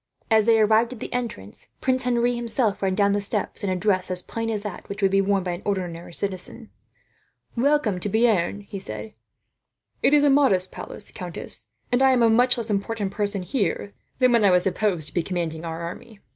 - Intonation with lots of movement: No, average, 4.1 semitones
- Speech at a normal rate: No, fast, 215 wpm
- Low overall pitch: No, high, 205 Hz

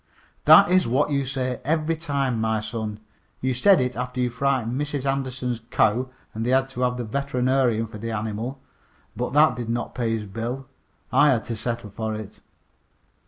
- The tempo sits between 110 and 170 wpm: No, average, 185 wpm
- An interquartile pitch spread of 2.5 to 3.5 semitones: Yes, average, 3.1 semitones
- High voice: No, low, 125 Hz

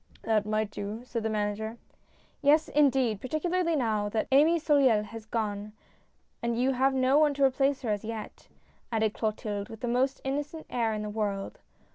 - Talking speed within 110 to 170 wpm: No, average, 185 wpm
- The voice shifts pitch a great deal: No, average, 4.2 semitones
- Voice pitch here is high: Yes, high, 230 Hz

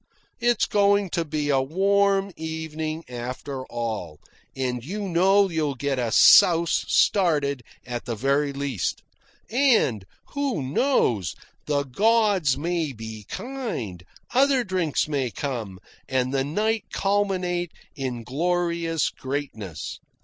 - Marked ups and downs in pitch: Yes, wide, 7.1 semitones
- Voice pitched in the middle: Yes, medium, 155 Hz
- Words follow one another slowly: Yes, slow, 120 wpm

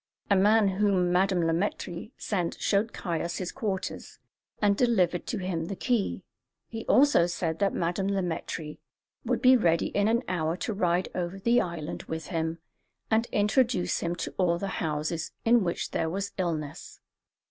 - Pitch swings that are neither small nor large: Yes, average, 3.5 semitones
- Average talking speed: Yes, average, 170 wpm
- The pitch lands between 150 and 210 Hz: Yes, medium, 185 Hz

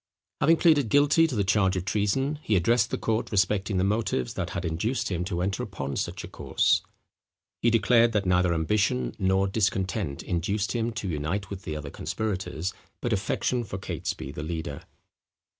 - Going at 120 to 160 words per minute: No, average, 175 wpm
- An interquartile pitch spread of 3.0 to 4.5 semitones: Yes, average, 4.2 semitones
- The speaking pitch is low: Yes, low, 100 Hz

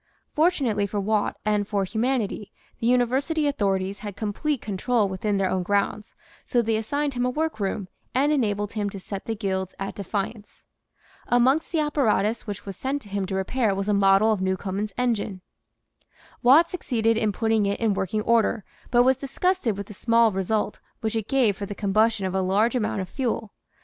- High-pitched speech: Yes, high, 215 Hz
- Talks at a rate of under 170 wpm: No, average, 185 wpm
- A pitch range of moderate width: Yes, average, 3.6 semitones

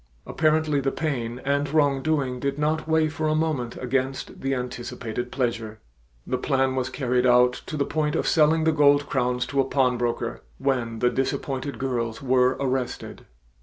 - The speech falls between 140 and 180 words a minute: Yes, average, 165 wpm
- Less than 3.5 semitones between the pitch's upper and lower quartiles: Yes, average, 2.9 semitones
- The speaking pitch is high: No, low, 135 Hz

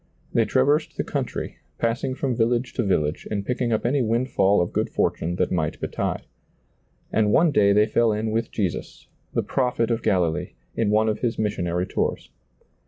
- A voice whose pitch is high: No, low, 110 Hz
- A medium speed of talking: Yes, average, 185 wpm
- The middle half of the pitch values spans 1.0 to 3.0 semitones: No, average, 3.4 semitones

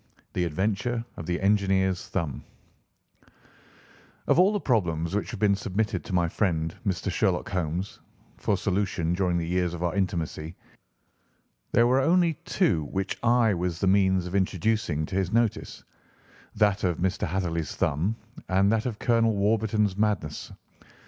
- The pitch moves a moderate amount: Yes, average, 3.6 semitones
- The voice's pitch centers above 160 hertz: No, very low, 95 Hz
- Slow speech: No, average, 150 wpm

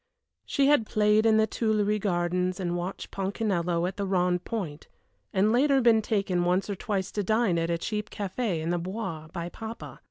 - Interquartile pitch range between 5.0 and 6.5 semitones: No, average, 3.7 semitones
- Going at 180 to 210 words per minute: Yes, average, 190 wpm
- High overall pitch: Yes, high, 195 Hz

